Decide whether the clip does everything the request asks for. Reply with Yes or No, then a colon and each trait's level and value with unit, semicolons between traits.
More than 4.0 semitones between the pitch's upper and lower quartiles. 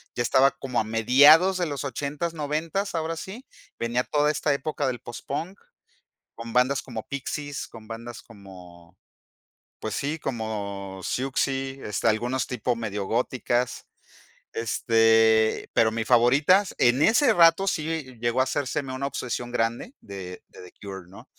Yes: average, 4.6 semitones